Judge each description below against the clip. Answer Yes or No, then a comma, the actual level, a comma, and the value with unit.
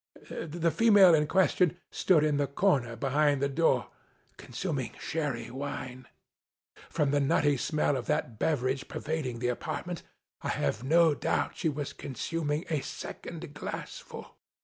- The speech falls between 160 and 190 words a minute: No, average, 145 wpm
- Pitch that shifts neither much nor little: Yes, average, 3.5 semitones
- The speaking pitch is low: No, medium, 145 Hz